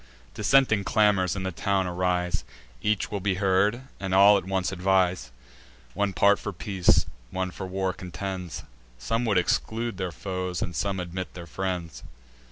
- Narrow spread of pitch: Yes, narrow, 1.8 semitones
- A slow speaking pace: No, average, 165 wpm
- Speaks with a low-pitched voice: Yes, very low, 95 Hz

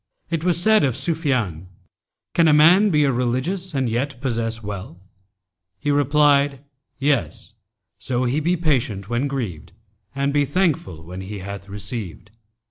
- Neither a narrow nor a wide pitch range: No, wide, 6.1 semitones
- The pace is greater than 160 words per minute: No, average, 150 wpm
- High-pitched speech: No, low, 135 Hz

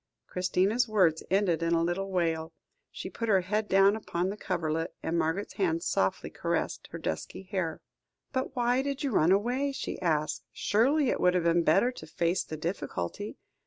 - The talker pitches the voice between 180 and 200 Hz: Yes, medium, 185 Hz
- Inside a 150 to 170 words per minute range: No, average, 180 wpm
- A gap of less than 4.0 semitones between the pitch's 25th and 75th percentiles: No, average, 4.5 semitones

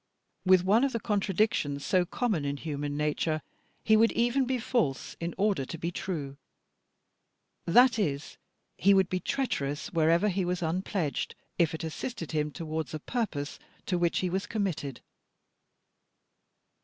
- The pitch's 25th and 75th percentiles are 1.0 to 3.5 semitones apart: No, wide, 5.4 semitones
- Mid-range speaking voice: Yes, medium, 175 Hz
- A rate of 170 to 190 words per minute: No, average, 150 wpm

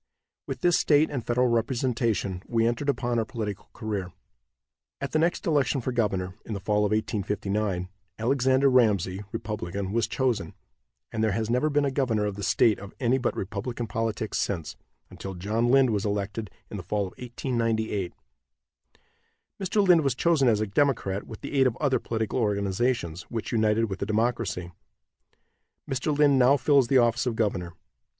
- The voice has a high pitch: No, low, 115 Hz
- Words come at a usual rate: Yes, average, 170 wpm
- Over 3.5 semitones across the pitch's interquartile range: Yes, average, 4.2 semitones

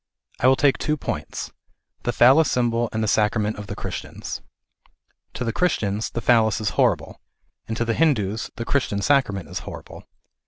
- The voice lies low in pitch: Yes, low, 115 Hz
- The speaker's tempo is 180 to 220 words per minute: No, average, 170 wpm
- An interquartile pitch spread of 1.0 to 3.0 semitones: No, average, 3.5 semitones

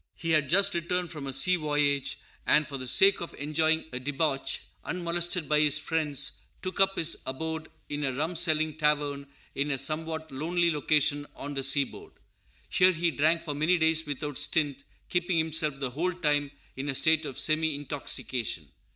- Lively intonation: No, narrow, 2.5 semitones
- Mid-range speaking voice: Yes, medium, 155 Hz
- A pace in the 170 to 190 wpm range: Yes, average, 175 wpm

